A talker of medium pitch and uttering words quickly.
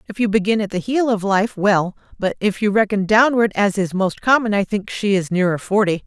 No: high, 205 Hz; fast, 235 wpm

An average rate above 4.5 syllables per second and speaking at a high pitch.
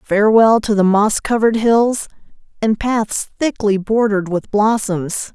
No: 4.4 syllables/s; high, 215 Hz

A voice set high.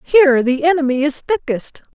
Yes: very high, 290 Hz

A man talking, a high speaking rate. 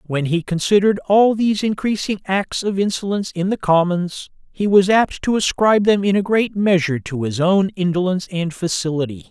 No: male; average, 180 wpm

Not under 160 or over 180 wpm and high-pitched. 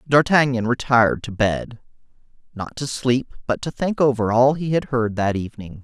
No: average, 165 wpm; low, 125 Hz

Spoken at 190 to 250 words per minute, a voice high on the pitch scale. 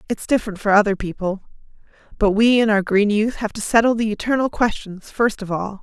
Yes: fast, 205 wpm; high, 210 Hz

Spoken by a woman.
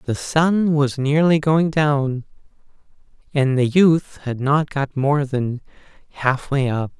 No: male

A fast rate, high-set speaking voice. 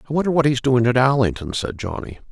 No: fast, 235 wpm; low, 125 Hz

